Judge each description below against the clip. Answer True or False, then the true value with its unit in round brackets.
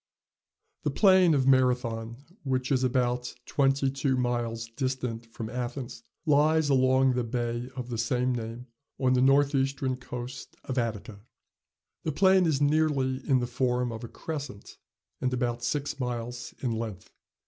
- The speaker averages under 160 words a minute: True (150 wpm)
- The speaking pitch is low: True (125 Hz)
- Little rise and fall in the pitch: True (2.2 semitones)